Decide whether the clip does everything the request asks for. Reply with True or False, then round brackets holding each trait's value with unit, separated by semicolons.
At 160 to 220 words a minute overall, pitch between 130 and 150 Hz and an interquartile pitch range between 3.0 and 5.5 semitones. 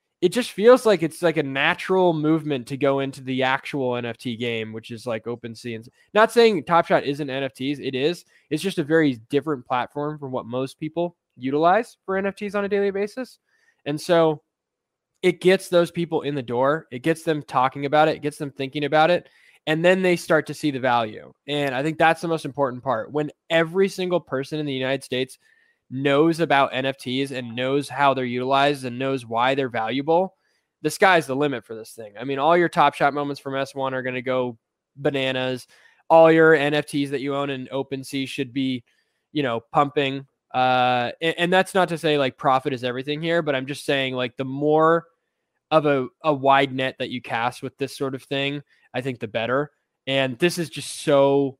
True (205 wpm; 140 Hz; 3.7 semitones)